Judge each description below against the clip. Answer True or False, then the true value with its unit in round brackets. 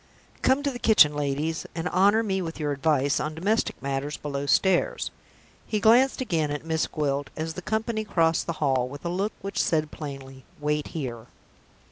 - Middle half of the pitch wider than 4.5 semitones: True (5.3 semitones)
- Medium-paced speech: True (180 wpm)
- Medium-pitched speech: True (160 Hz)